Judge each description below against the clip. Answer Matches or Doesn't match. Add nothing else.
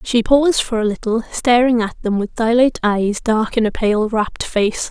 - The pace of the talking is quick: Matches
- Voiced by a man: Doesn't match